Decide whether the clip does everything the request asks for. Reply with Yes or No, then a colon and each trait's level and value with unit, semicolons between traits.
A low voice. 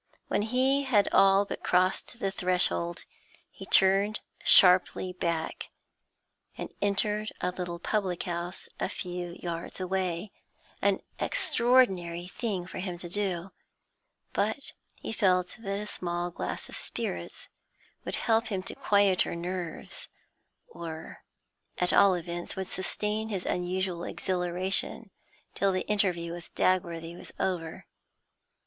No: medium, 185 Hz